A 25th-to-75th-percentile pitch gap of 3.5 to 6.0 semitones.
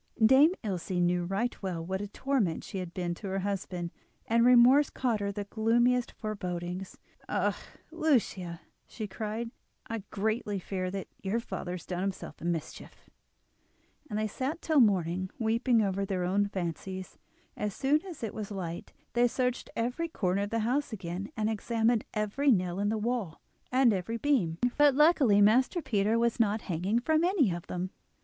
Yes: average, 4.5 semitones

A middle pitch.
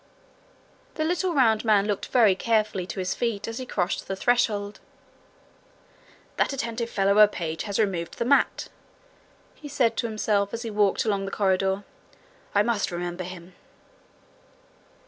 No: high, 210 Hz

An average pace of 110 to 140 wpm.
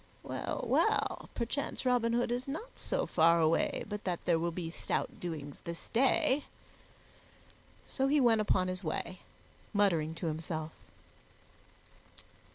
Yes: slow, 135 wpm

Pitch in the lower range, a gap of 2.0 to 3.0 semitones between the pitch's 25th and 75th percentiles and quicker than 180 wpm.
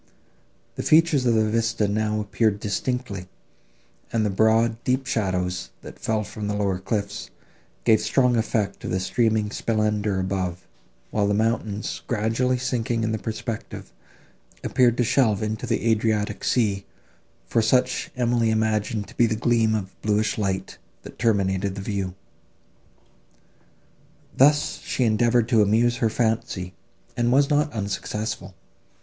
No: low, 110 Hz; narrow, 2.5 semitones; average, 140 wpm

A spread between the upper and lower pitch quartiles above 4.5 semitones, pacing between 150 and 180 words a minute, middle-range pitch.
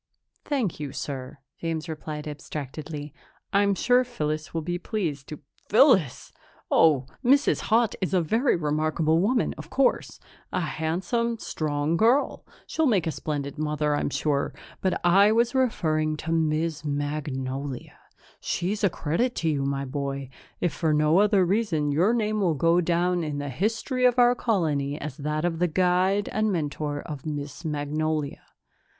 Yes: average, 5.2 semitones; average, 155 wpm; medium, 160 Hz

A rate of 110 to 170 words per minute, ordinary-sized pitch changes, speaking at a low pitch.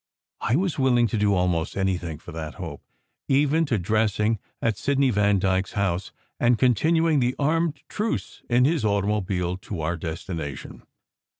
No: average, 155 wpm; wide, 6.7 semitones; low, 105 Hz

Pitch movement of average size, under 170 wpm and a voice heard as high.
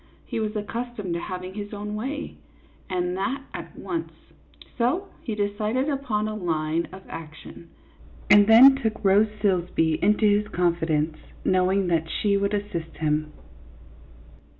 Yes: average, 4.0 semitones; average, 140 wpm; high, 205 Hz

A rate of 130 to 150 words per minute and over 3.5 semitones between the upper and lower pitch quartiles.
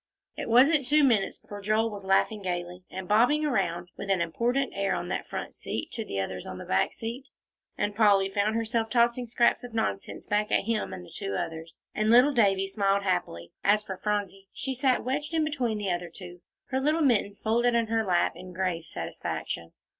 No: fast, 205 wpm; average, 4.5 semitones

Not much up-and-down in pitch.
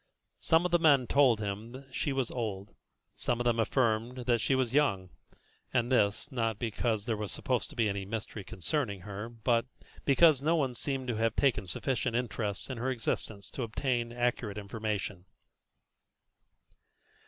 No: average, 3.5 semitones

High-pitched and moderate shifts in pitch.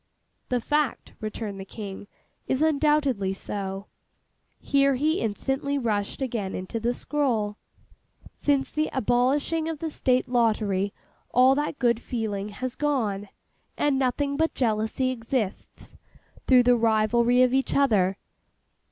Yes: high, 245 Hz; average, 4.6 semitones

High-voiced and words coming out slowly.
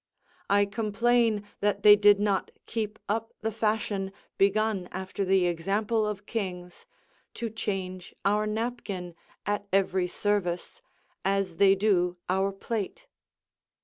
Yes: high, 200 Hz; slow, 120 wpm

